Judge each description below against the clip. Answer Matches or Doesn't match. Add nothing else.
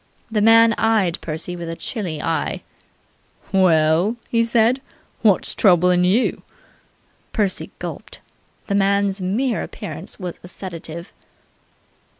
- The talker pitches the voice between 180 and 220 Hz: Matches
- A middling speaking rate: Doesn't match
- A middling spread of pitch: Matches